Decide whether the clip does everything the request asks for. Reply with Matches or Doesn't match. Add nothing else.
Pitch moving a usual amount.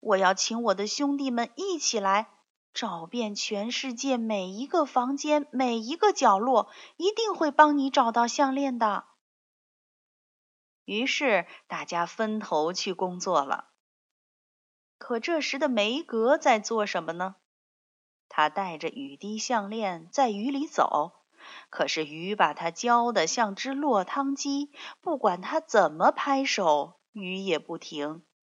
Doesn't match